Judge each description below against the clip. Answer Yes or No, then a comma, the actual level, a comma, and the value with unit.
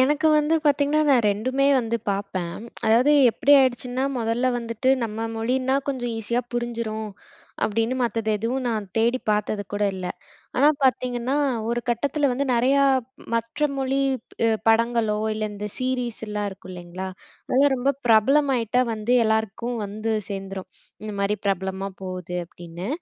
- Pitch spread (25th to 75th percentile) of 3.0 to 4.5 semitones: Yes, average, 3.5 semitones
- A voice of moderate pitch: No, high, 230 Hz